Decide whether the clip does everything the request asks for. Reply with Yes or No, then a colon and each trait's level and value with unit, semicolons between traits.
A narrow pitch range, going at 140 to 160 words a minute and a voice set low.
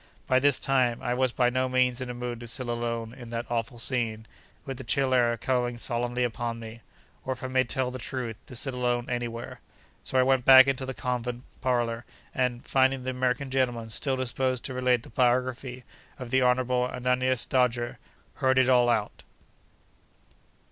No: narrow, 1.4 semitones; average, 185 wpm; low, 125 Hz